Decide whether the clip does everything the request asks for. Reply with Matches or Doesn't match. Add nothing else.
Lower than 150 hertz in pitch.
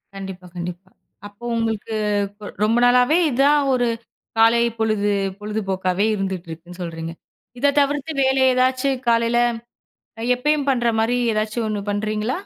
Doesn't match